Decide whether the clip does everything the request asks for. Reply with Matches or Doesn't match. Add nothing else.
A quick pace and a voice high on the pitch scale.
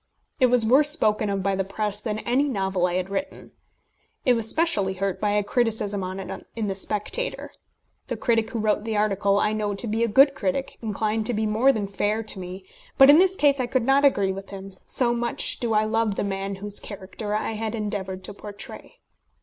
Matches